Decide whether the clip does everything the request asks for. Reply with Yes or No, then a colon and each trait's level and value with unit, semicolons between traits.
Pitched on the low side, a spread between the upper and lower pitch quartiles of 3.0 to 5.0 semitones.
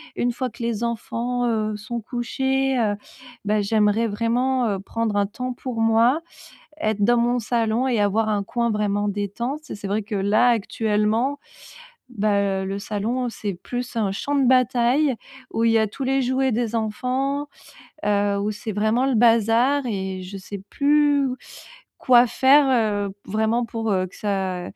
No: high, 225 Hz; average, 3.3 semitones